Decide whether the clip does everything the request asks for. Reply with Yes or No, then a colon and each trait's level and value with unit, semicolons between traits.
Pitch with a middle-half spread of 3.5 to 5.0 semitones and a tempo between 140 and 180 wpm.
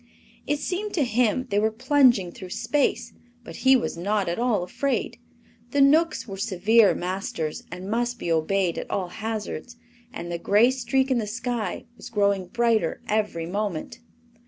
Yes: average, 4.6 semitones; average, 165 wpm